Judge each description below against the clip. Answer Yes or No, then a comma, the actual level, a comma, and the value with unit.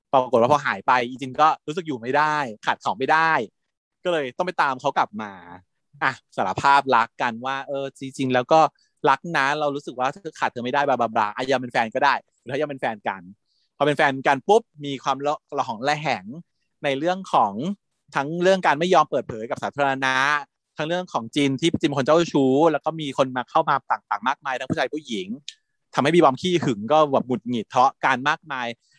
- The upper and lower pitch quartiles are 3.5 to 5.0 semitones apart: No, average, 3.1 semitones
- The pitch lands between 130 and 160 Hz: Yes, medium, 140 Hz